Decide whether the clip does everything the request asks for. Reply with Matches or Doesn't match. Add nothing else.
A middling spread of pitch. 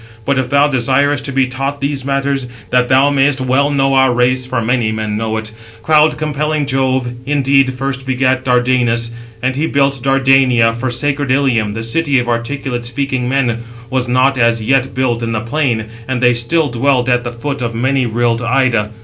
Doesn't match